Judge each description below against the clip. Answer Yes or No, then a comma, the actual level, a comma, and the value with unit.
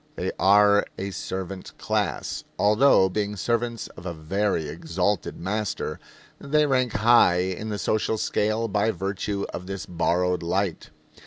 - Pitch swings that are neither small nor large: Yes, average, 3.0 semitones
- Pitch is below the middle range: Yes, low, 100 Hz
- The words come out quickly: No, average, 140 wpm